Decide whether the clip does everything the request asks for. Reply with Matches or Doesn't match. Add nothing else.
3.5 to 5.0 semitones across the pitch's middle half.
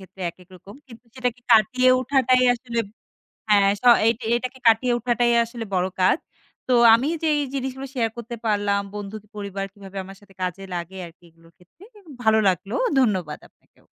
Matches